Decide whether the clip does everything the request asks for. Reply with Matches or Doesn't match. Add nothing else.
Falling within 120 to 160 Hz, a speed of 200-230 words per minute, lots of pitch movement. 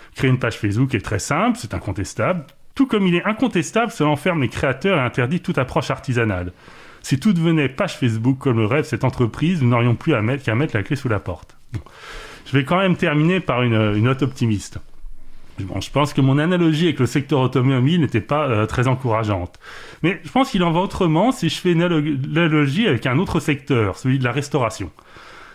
Matches